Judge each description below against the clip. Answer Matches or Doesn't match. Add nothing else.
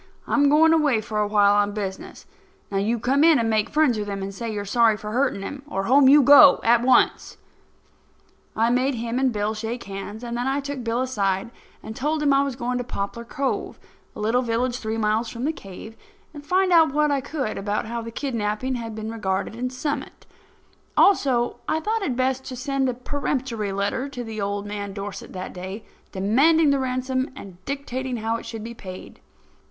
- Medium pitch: Doesn't match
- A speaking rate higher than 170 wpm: Matches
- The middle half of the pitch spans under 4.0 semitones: Doesn't match